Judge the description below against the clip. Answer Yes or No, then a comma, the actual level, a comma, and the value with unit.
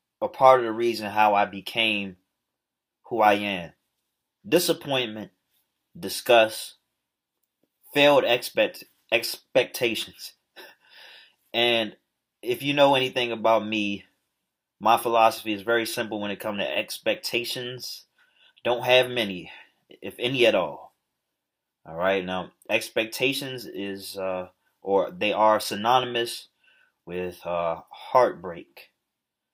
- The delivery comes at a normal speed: No, slow, 110 wpm